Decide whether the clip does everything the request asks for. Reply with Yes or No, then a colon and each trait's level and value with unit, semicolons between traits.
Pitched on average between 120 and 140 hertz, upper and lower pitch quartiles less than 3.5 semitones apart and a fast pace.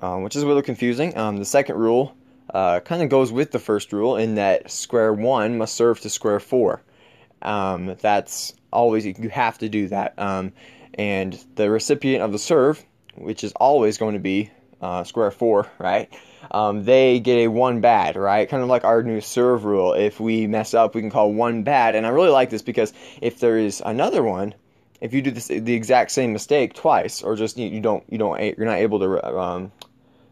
No: low, 110 Hz; average, 3.0 semitones; fast, 210 wpm